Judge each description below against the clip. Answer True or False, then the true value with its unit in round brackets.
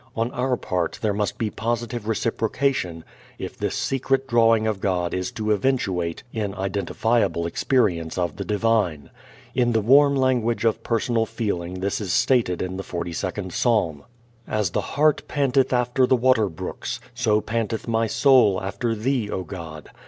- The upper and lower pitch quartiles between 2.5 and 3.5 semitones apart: False (4.5 semitones)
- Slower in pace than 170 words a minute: True (160 wpm)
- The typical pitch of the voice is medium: False (110 Hz)